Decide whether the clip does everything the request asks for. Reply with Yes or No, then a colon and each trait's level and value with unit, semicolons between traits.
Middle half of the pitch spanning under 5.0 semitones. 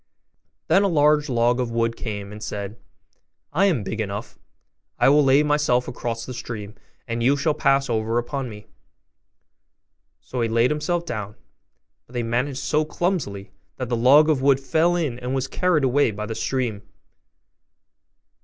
Yes: average, 4.4 semitones